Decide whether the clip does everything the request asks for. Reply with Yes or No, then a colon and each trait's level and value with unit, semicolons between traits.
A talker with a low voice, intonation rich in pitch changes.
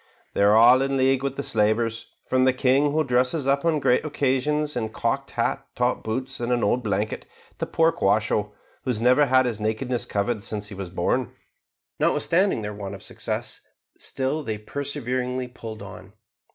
No: low, 125 Hz; average, 3.8 semitones